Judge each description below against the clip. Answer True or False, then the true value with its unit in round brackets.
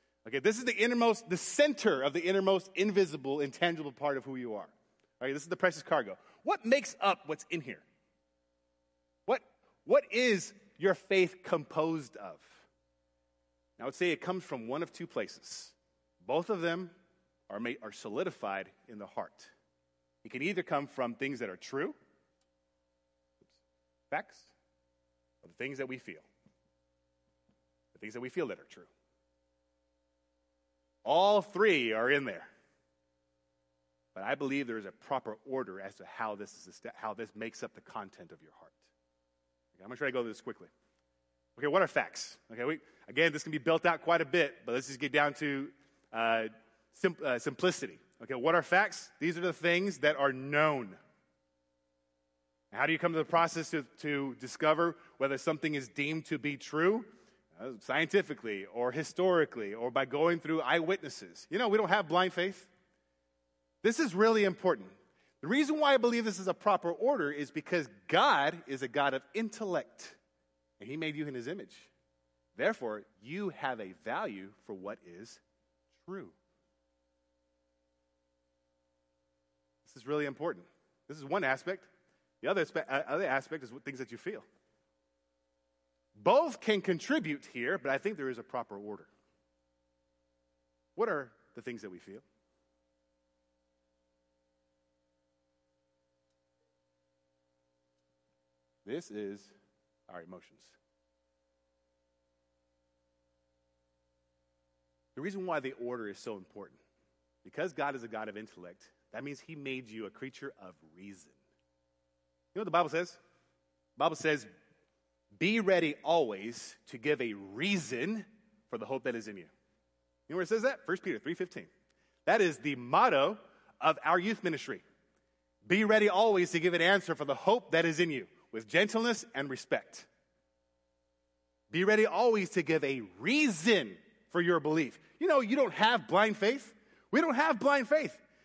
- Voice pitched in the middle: False (125 Hz)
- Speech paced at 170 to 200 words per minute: False (160 wpm)